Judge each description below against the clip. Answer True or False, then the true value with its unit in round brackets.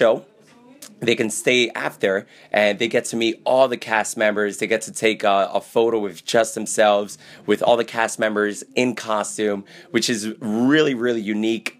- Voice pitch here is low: True (110 Hz)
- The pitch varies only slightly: True (2.1 semitones)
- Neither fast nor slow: True (185 wpm)